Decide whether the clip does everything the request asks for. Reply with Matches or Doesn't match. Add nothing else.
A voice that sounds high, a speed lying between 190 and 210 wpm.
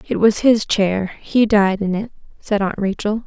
Matches